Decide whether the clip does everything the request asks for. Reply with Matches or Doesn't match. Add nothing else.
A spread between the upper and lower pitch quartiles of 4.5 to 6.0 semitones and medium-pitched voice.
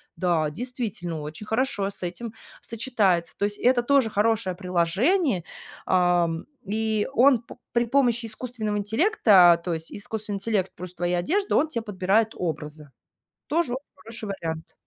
Doesn't match